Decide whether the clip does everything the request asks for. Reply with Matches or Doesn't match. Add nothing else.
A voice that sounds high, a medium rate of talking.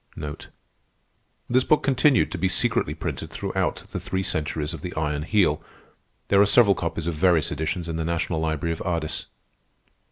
Doesn't match